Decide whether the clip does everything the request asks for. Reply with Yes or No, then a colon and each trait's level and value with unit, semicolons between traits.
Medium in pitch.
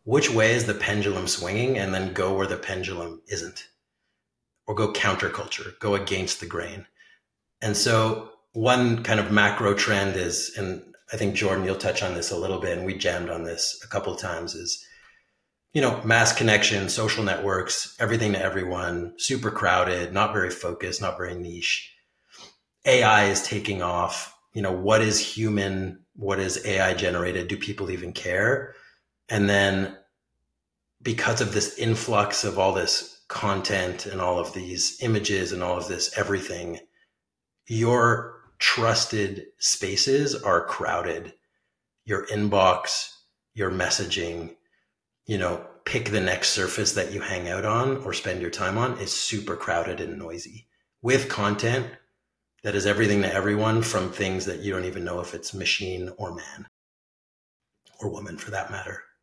No: low, 100 Hz